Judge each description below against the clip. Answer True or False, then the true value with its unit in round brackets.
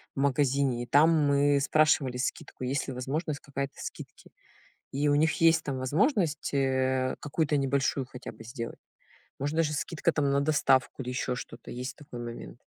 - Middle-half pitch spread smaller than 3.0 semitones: True (2.4 semitones)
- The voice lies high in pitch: False (140 Hz)